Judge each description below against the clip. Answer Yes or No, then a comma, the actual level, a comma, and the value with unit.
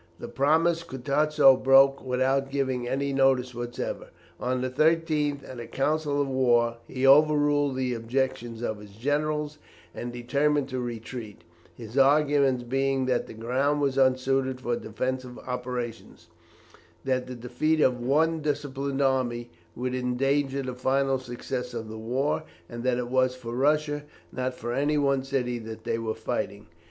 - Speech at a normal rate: Yes, average, 155 wpm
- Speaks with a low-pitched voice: Yes, low, 130 Hz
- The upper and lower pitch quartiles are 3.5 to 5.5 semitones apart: No, narrow, 2.4 semitones